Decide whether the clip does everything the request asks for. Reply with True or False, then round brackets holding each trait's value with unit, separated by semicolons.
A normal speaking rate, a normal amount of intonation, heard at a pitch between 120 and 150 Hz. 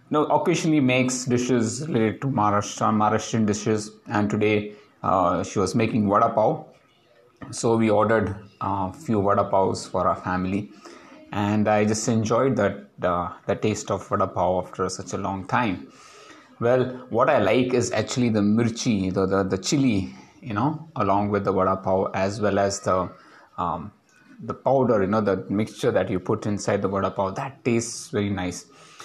False (175 wpm; 3.1 semitones; 105 Hz)